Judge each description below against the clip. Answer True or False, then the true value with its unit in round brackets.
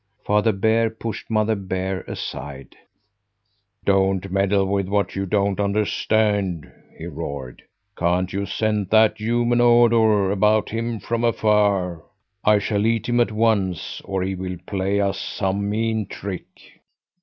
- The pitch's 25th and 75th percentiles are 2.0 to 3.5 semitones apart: True (2.5 semitones)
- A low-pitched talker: True (100 Hz)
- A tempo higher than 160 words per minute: False (135 wpm)